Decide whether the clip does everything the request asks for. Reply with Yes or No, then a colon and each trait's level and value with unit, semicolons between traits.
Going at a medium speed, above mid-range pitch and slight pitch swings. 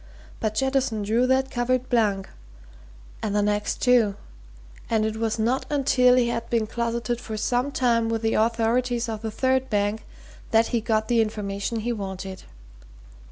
Yes: average, 160 wpm; high, 230 Hz; narrow, 2.3 semitones